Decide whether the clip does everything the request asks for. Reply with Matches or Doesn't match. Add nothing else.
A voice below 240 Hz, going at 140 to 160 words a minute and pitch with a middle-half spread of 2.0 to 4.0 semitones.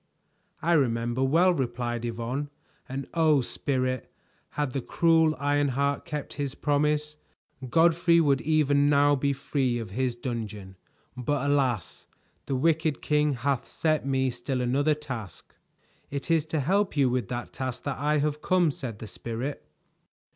Matches